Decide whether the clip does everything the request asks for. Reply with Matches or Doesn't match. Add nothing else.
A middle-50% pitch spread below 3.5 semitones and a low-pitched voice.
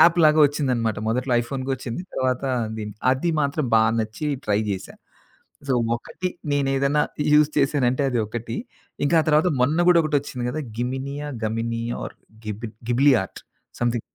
Doesn't match